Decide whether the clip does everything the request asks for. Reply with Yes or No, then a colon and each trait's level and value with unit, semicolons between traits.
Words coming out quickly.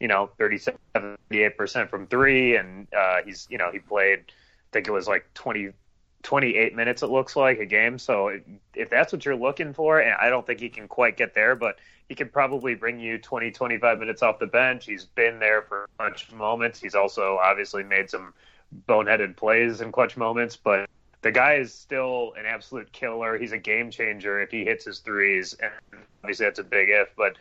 Yes: fast, 210 wpm